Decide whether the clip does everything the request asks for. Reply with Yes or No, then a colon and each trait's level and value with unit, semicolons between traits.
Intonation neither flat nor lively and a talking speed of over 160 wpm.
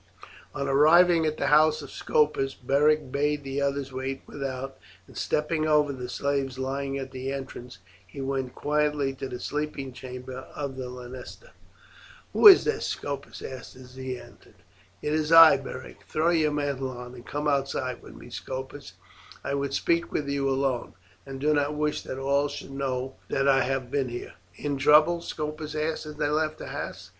No: narrow, 2.2 semitones; average, 180 wpm